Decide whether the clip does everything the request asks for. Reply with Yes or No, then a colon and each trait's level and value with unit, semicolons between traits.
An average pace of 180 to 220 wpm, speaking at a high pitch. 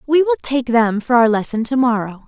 No: fast, 240 wpm; high, 235 Hz